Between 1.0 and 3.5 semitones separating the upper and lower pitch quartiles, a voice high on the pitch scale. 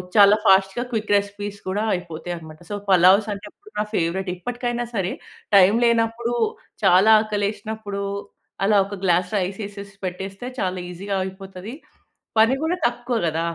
Yes: average, 2.8 semitones; high, 200 Hz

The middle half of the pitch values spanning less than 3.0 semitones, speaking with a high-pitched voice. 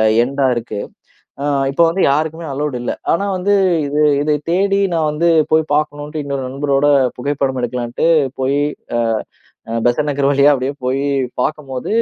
No: narrow, 2.5 semitones; medium, 145 Hz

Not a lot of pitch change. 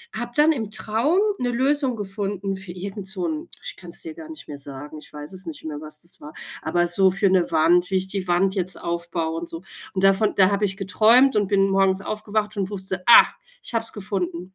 No: average, 3.4 semitones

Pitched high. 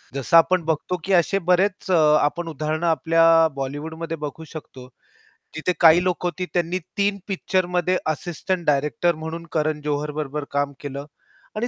No: medium, 165 Hz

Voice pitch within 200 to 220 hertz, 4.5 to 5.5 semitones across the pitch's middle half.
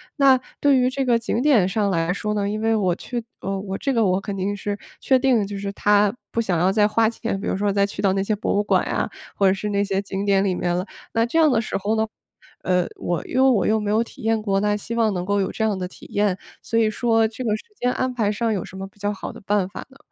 No: high, 205 Hz; average, 2.7 semitones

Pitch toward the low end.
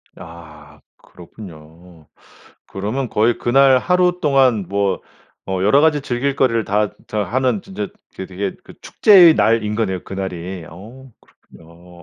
Yes: low, 105 Hz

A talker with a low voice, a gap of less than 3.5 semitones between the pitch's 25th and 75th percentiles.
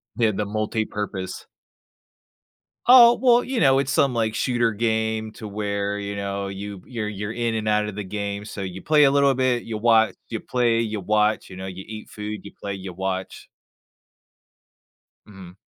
Yes: low, 105 Hz; narrow, 2.5 semitones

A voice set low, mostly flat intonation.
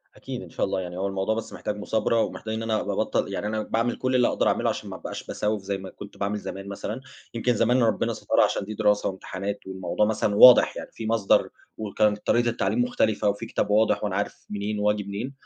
Yes: low, 105 Hz; narrow, 2.0 semitones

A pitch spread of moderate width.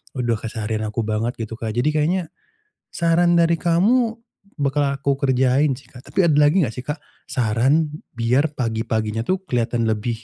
No: wide, 5.8 semitones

